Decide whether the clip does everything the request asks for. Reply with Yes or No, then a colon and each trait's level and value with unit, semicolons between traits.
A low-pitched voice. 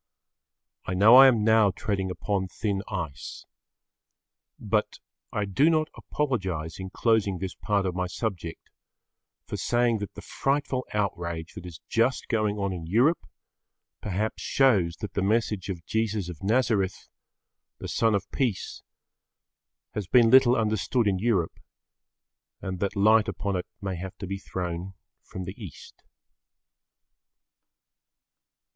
Yes: low, 100 Hz